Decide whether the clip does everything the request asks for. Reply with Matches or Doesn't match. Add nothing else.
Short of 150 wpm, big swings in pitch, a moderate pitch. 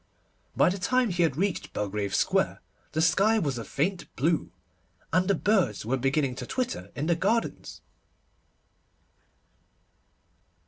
Matches